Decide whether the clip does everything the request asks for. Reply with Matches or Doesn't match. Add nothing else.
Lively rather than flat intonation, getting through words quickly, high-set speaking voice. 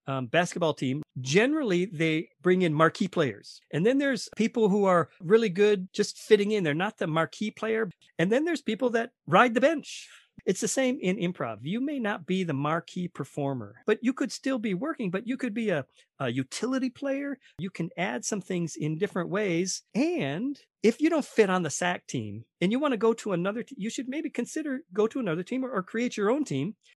Matches